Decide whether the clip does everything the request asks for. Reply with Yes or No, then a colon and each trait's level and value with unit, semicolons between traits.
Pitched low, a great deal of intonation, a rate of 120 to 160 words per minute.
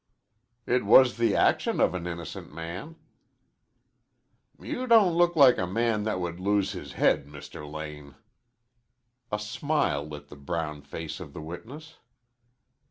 Yes: very low, 90 Hz; wide, 8.3 semitones; average, 140 wpm